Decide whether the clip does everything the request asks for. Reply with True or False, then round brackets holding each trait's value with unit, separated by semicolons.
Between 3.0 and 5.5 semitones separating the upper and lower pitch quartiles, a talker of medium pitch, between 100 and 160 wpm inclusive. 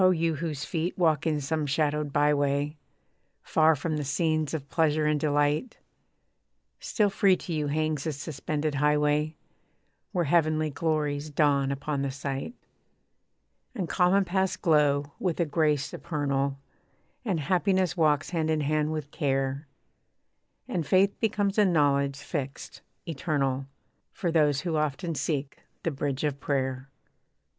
False (2.6 semitones; 150 Hz; 140 wpm)